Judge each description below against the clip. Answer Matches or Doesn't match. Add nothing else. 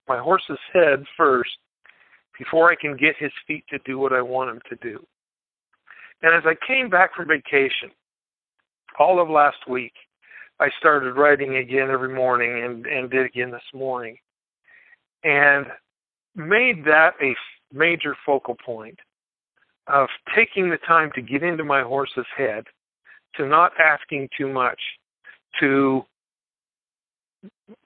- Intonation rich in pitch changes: Doesn't match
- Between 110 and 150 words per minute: Matches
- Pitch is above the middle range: Doesn't match